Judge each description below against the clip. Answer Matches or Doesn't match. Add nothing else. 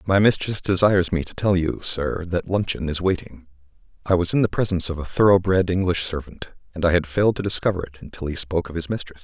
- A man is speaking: Matches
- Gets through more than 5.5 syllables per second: Matches